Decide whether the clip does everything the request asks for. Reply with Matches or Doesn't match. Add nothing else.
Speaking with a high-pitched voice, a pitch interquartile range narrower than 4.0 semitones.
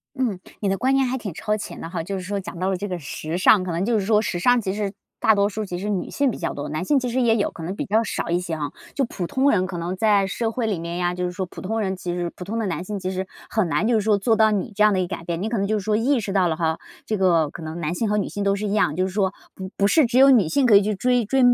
Matches